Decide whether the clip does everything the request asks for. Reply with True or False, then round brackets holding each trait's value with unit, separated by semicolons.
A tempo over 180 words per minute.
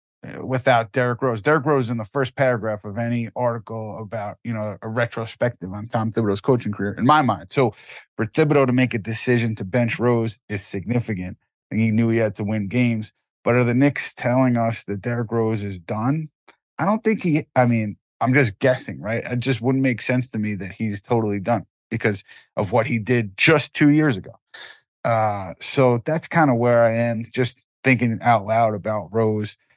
True (200 wpm)